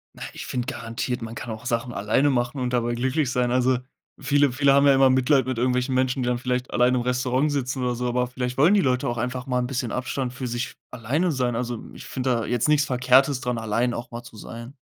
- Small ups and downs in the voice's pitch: Yes, narrow, 1.3 semitones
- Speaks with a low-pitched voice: Yes, low, 125 Hz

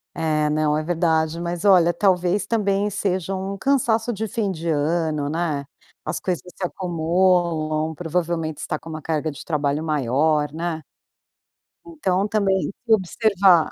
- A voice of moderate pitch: Yes, medium, 170 Hz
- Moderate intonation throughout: Yes, average, 3.6 semitones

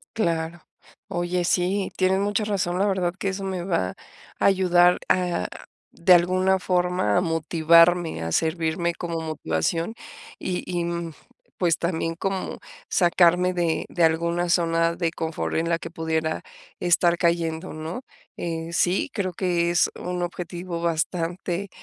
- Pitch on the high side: No, medium, 175 Hz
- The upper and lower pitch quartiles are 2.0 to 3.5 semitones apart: No, narrow, 1.6 semitones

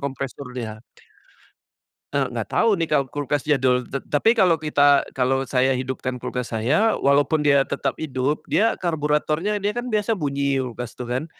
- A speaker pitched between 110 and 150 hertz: Yes, medium, 140 Hz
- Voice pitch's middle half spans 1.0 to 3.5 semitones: Yes, average, 3.2 semitones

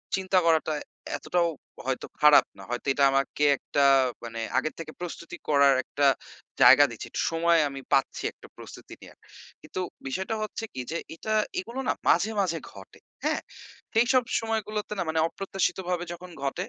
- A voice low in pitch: No, medium, 170 Hz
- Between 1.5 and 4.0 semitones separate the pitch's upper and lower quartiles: No, average, 5.3 semitones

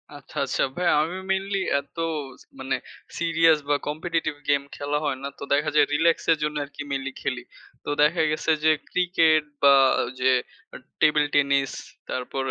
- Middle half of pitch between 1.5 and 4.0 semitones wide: Yes, average, 2.9 semitones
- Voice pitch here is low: No, medium, 150 Hz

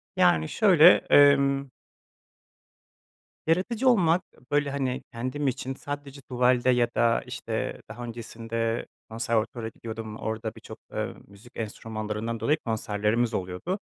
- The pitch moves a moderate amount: Yes, average, 4.0 semitones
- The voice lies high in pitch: No, low, 120 Hz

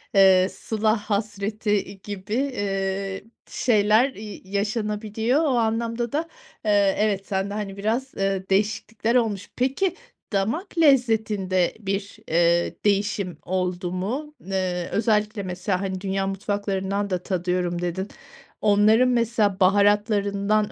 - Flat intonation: Yes, narrow, 2.3 semitones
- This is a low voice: No, high, 205 Hz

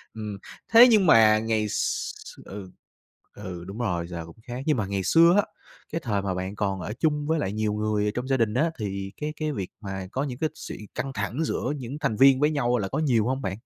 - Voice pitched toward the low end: Yes, low, 110 Hz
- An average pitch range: No, wide, 6.0 semitones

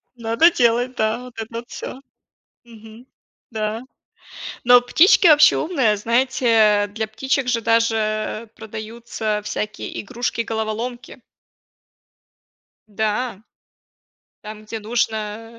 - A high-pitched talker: Yes, high, 225 Hz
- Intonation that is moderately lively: No, narrow, 2.1 semitones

